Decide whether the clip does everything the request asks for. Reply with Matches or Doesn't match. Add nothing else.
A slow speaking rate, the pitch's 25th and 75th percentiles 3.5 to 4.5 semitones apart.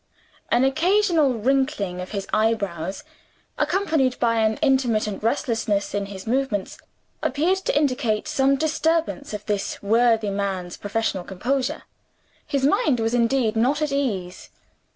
Doesn't match